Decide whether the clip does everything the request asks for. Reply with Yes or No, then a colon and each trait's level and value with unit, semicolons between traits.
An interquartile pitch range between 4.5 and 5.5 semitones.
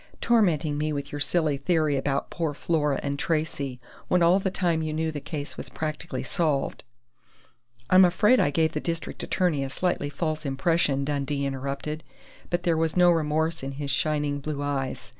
No: average, 2.9 semitones